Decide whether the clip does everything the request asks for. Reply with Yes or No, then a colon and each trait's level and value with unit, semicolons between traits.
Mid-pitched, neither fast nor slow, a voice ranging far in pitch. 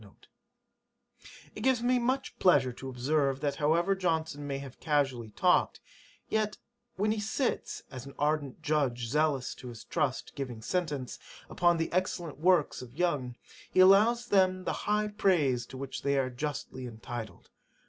Yes: medium, 150 Hz; average, 160 wpm; wide, 6.0 semitones